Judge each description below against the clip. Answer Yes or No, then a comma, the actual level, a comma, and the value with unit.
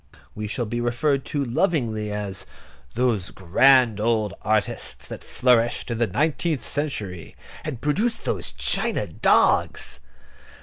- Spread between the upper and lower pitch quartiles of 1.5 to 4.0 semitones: No, average, 4.7 semitones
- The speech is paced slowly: Yes, slow, 125 wpm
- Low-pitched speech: Yes, low, 120 Hz